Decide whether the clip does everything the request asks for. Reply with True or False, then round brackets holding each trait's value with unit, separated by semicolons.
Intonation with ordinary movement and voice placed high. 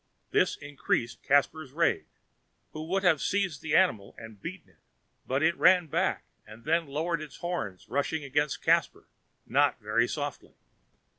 False (4.1 semitones; 150 Hz)